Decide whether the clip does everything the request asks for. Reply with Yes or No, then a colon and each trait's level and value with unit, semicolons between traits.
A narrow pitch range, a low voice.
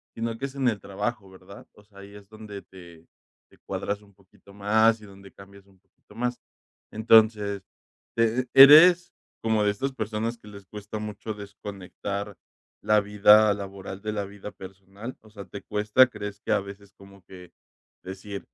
Yes: narrow, 1.8 semitones; low, 105 Hz